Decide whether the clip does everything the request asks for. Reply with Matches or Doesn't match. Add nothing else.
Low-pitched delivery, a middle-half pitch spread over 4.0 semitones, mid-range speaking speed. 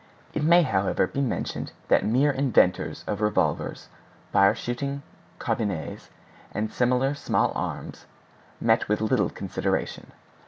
Doesn't match